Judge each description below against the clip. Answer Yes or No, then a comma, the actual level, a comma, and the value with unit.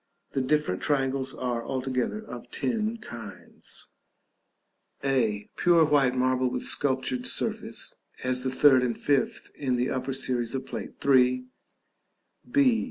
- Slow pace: Yes, slow, 130 wpm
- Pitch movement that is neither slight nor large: No, narrow, 2.0 semitones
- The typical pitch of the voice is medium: No, low, 130 Hz